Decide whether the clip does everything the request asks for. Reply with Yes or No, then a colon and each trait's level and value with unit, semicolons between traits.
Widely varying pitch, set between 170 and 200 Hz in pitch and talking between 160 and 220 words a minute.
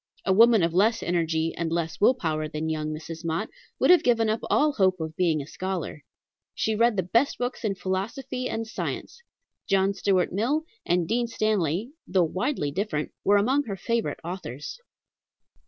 Yes: wide, 5.7 semitones; high, 190 Hz; average, 175 wpm